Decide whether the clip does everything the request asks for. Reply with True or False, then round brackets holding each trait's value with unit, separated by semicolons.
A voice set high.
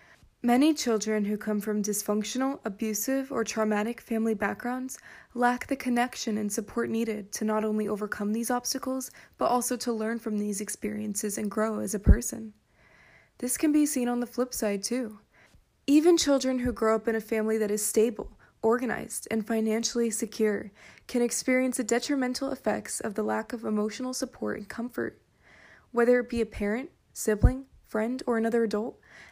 True (225 Hz)